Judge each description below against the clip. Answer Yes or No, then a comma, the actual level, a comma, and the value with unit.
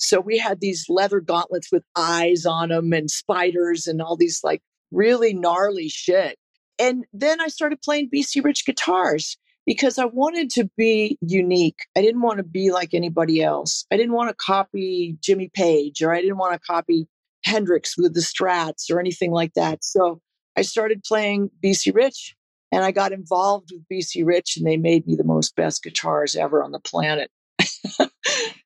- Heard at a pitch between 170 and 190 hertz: Yes, medium, 185 Hz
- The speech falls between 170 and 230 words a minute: Yes, average, 180 wpm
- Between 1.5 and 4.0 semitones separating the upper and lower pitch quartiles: No, average, 4.9 semitones